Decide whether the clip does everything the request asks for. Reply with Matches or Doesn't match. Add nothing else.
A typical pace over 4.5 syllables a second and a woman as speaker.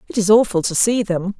Matches